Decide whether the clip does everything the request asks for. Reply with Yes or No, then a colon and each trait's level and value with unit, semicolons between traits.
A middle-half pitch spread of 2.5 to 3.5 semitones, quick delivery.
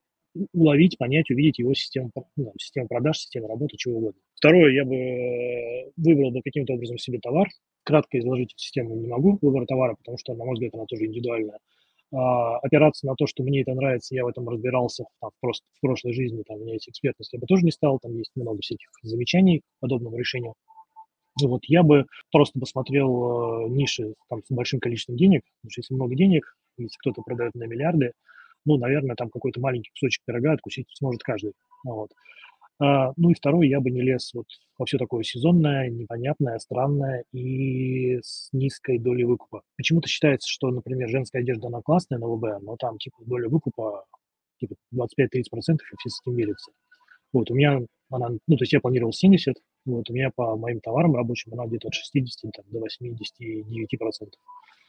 Yes: average, 3.2 semitones; fast, 185 wpm